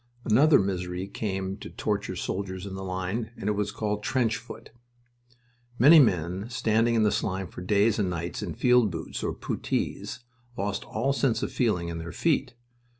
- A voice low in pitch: Yes, low, 105 Hz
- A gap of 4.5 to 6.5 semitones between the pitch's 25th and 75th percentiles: No, average, 3.7 semitones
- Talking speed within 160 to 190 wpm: Yes, average, 170 wpm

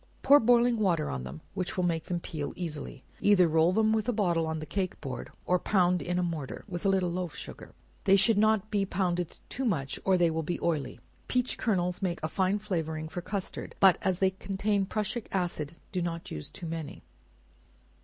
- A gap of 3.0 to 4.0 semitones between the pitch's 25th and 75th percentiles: Yes, average, 3.4 semitones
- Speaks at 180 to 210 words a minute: Yes, fast, 205 wpm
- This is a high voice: No, medium, 180 Hz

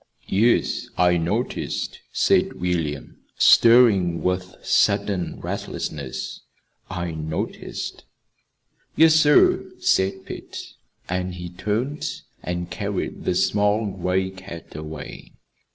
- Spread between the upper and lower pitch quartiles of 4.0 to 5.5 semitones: No, average, 3.0 semitones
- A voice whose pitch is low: Yes, very low, 90 Hz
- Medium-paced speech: No, slow, 95 wpm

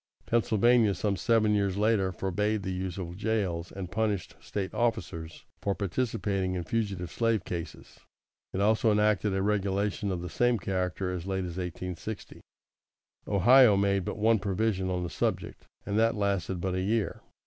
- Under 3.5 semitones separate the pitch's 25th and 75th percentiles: Yes, average, 2.8 semitones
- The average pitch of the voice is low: Yes, low, 100 Hz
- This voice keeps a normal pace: Yes, average, 160 wpm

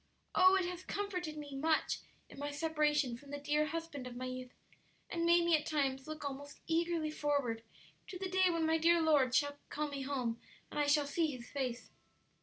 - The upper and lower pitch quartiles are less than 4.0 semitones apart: Yes, average, 3.2 semitones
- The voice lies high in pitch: Yes, very high, 295 Hz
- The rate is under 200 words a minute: No, fast, 205 wpm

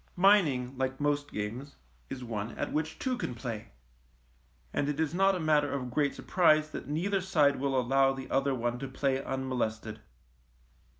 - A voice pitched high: No, low, 135 Hz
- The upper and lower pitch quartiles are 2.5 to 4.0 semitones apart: Yes, average, 3.4 semitones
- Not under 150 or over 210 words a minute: Yes, average, 170 wpm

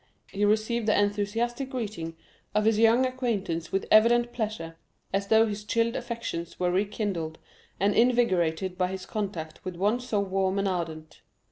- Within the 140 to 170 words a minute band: Yes, average, 155 wpm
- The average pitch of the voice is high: Yes, high, 205 Hz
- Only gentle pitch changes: No, average, 3.9 semitones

